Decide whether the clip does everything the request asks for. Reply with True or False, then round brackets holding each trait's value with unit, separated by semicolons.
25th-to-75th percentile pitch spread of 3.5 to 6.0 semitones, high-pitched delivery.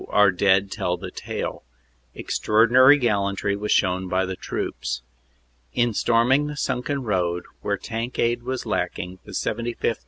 False (4.3 semitones; 105 Hz)